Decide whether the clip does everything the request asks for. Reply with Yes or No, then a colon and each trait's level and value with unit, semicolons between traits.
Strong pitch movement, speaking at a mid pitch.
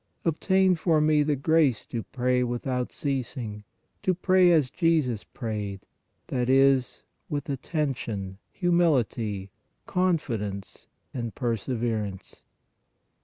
No: wide, 5.7 semitones; low, 130 Hz